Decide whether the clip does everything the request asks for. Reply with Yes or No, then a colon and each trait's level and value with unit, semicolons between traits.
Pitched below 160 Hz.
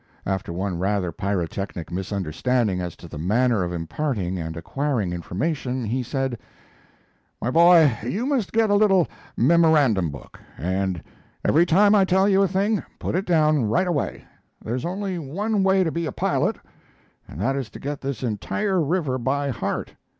Yes: low, 135 Hz